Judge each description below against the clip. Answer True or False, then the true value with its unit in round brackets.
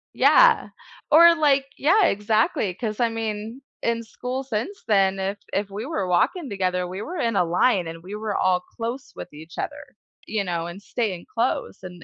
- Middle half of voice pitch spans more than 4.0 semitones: True (5.1 semitones)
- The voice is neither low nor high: False (210 Hz)